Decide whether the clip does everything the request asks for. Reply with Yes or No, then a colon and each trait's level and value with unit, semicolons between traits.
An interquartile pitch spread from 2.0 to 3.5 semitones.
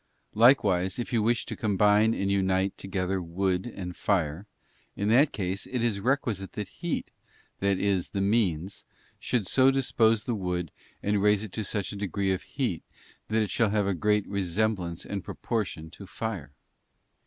Yes: average, 2.8 semitones